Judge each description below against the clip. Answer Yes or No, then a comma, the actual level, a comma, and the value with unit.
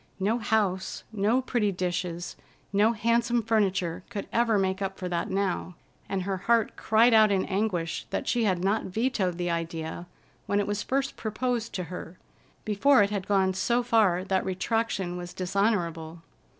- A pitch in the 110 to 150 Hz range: No, high, 200 Hz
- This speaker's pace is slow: No, average, 165 wpm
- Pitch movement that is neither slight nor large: Yes, average, 3.5 semitones